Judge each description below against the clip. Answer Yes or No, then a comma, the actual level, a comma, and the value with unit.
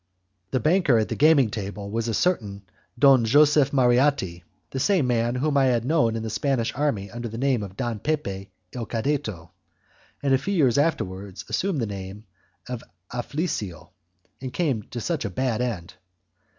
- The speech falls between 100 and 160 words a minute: No, average, 175 wpm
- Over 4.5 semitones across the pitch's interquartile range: Yes, average, 5.2 semitones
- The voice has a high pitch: No, low, 120 Hz